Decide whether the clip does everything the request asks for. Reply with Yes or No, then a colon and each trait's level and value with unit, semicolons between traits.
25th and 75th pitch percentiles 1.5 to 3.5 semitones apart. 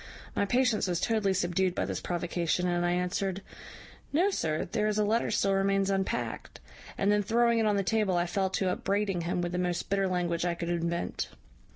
Yes: average, 2.9 semitones